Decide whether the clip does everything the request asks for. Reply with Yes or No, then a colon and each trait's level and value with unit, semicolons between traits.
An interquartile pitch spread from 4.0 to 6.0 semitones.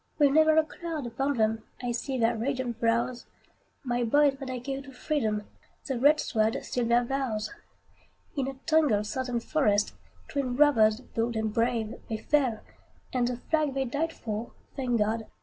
No: average, 3.5 semitones